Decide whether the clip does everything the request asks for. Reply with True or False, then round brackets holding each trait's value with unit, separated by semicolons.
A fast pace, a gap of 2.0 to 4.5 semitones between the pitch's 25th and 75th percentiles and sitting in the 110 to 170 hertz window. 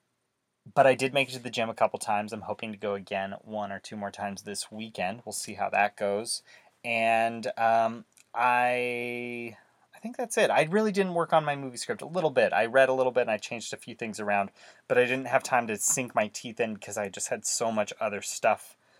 True (240 wpm; 3.4 semitones; 115 Hz)